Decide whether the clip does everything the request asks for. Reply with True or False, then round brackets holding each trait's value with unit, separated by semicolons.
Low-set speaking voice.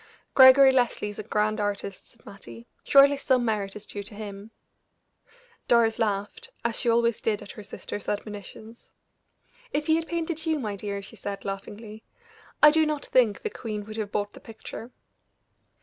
False (220 Hz)